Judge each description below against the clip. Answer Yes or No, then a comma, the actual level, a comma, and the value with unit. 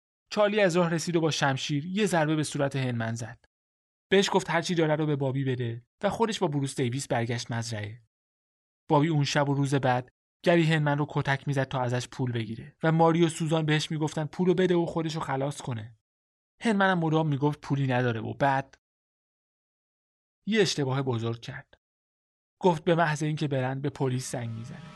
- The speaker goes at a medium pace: No, fast, 185 wpm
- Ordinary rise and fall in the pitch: Yes, average, 4.7 semitones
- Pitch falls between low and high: Yes, medium, 145 Hz